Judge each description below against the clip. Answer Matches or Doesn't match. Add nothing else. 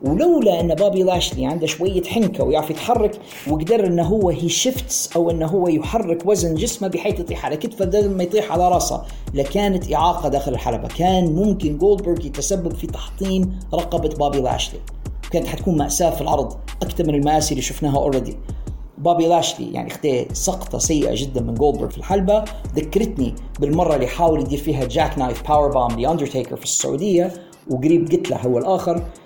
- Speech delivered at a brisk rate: Matches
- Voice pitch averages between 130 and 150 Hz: Doesn't match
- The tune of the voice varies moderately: Matches